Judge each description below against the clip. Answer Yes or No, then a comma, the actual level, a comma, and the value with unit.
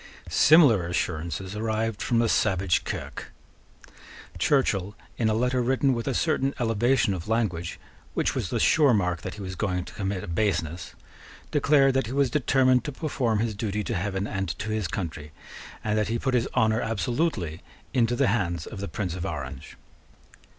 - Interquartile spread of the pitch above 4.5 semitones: Yes, average, 5.2 semitones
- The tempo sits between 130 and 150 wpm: No, average, 180 wpm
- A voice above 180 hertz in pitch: No, low, 110 Hz